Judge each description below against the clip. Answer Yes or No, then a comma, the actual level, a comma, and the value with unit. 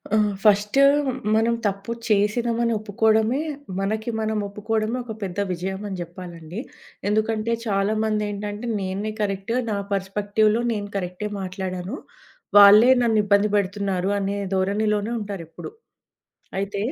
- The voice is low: No, high, 205 Hz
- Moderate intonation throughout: No, narrow, 1.9 semitones